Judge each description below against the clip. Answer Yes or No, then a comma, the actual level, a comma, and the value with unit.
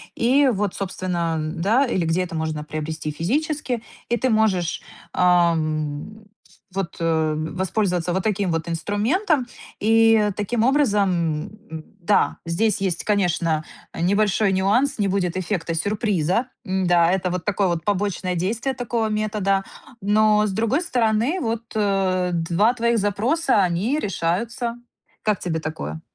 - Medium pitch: No, high, 195 Hz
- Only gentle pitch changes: No, average, 4.6 semitones